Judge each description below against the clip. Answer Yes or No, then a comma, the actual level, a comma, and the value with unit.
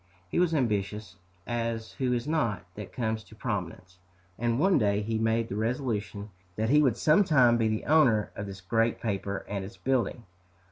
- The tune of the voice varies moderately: Yes, average, 3.4 semitones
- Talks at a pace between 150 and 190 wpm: Yes, average, 180 wpm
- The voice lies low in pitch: Yes, low, 110 Hz